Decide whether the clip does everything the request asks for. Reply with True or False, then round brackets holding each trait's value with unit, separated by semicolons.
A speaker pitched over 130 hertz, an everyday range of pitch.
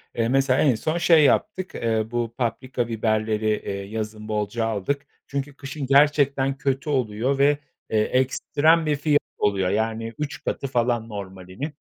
False (125 Hz; 4.3 semitones)